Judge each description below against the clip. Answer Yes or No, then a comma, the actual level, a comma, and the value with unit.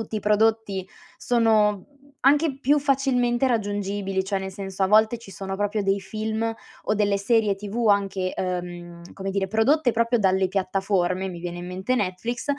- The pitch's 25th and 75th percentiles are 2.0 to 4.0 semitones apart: Yes, average, 2.9 semitones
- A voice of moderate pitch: No, high, 205 Hz